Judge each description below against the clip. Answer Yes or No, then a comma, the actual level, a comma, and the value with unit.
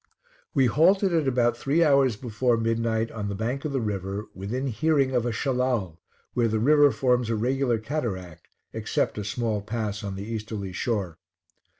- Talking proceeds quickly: No, average, 175 wpm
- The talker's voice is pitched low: Yes, low, 115 Hz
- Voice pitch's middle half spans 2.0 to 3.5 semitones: No, average, 4.1 semitones